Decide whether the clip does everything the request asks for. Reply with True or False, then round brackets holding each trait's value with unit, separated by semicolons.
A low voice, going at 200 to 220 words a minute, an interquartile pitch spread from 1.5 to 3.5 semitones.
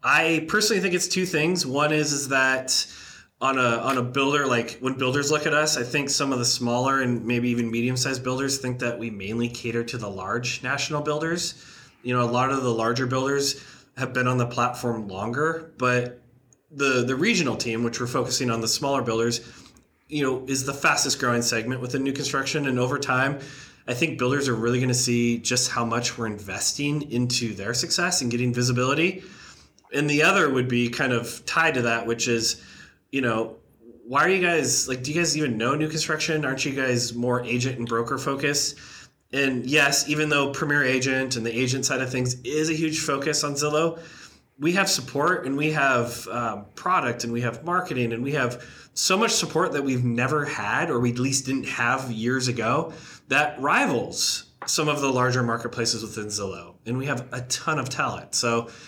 True (130 Hz; 205 wpm; 3.2 semitones)